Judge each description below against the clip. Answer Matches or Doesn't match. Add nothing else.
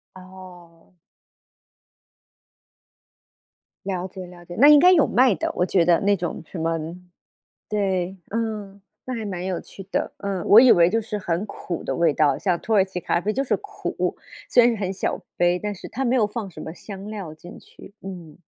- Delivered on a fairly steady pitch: Doesn't match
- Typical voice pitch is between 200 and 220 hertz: Doesn't match